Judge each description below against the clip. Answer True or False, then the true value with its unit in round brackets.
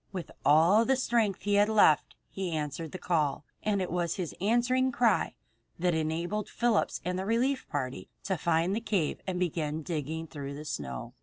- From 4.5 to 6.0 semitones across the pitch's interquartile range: True (5.1 semitones)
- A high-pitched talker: False (180 Hz)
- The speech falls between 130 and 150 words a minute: False (180 wpm)